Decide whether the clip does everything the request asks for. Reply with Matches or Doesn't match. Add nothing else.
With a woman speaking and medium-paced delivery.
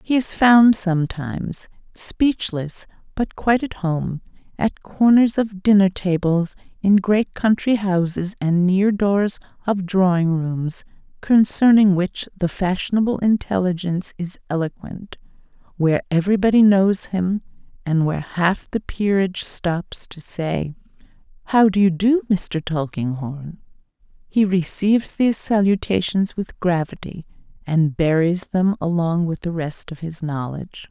Doesn't match